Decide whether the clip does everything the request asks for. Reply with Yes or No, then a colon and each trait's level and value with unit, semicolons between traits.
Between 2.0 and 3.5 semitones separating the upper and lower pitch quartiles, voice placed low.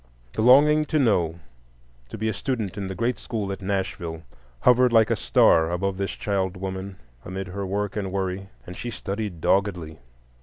Yes: average, 2.8 semitones; low, 100 Hz